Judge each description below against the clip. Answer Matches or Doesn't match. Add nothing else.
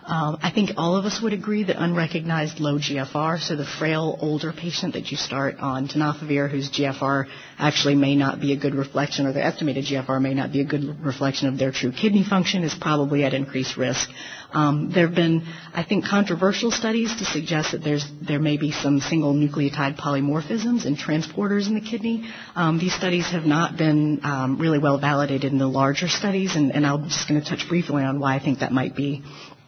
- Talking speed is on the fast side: Matches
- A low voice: Doesn't match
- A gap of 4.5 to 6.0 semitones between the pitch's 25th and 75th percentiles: Doesn't match